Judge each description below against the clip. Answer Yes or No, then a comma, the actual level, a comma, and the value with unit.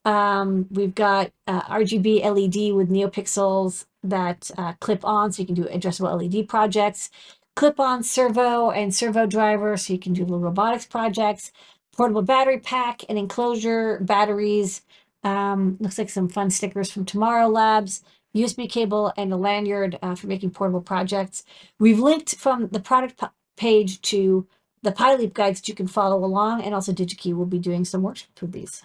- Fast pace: No, average, 175 wpm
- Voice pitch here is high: Yes, high, 205 Hz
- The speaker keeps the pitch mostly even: Yes, narrow, 2.2 semitones